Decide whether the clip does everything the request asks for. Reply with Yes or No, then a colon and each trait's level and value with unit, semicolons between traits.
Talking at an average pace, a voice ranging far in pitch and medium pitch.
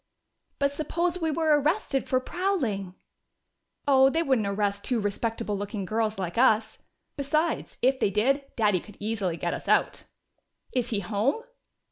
No: average, 150 wpm; wide, 5.7 semitones; high, 235 Hz